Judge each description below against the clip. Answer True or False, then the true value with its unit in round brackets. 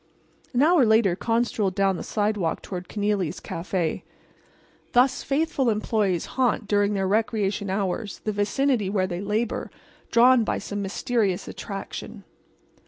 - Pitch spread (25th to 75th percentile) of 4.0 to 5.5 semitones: False (3.3 semitones)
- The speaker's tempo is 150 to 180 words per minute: False (135 wpm)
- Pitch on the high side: True (210 Hz)